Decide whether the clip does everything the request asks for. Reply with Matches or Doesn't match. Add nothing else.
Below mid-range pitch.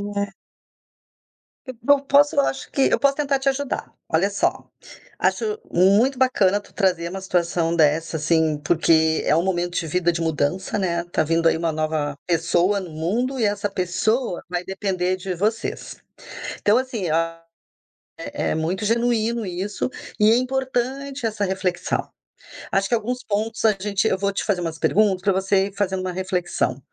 Doesn't match